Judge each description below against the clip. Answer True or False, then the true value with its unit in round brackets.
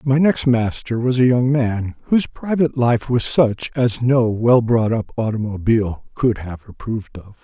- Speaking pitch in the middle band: False (120 Hz)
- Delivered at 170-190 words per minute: True (175 wpm)